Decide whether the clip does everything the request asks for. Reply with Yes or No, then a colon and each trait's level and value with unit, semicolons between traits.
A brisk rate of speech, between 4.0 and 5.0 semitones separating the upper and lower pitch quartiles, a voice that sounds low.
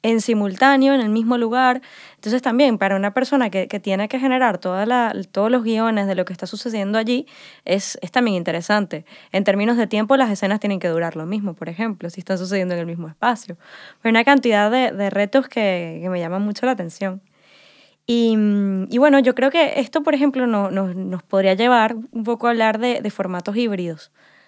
No: fast, 210 wpm; average, 4.4 semitones; high, 215 Hz